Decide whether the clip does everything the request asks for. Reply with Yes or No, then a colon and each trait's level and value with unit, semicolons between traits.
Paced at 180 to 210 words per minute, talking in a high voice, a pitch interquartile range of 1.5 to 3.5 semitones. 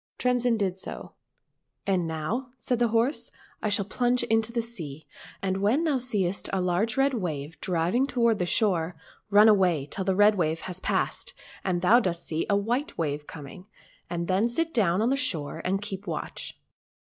No: average, 190 wpm; high, 200 Hz; average, 5.2 semitones